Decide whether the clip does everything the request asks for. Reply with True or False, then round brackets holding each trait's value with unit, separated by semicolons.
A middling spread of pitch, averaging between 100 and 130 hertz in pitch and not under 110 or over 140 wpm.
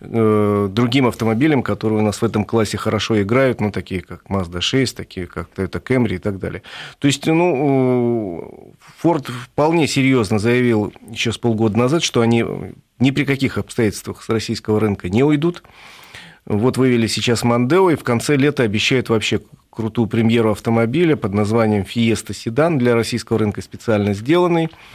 False (3.5 semitones; 115 Hz; 160 wpm)